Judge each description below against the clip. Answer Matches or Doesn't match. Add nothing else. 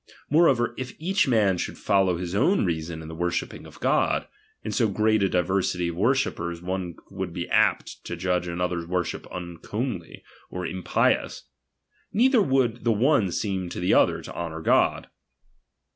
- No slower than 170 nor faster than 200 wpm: Doesn't match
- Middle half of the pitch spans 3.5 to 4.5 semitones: Doesn't match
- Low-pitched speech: Matches